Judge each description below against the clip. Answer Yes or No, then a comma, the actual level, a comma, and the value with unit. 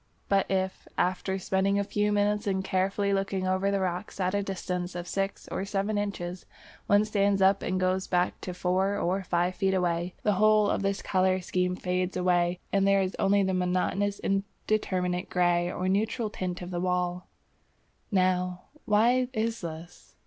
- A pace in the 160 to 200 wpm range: Yes, average, 175 wpm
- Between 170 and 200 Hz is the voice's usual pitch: Yes, high, 190 Hz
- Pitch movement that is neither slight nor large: No, narrow, 1.7 semitones